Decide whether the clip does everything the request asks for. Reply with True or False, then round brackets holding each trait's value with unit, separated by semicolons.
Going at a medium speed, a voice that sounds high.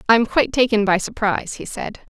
True (195 wpm; 220 Hz)